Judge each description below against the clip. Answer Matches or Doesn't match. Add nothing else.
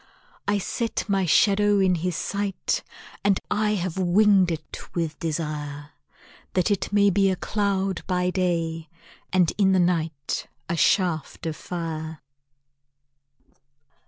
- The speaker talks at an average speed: Doesn't match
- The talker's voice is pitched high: Doesn't match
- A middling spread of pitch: Matches